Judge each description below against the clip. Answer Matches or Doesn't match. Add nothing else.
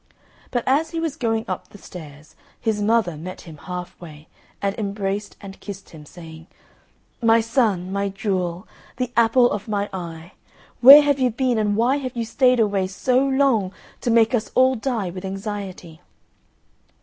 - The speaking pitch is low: Doesn't match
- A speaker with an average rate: Matches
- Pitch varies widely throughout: Doesn't match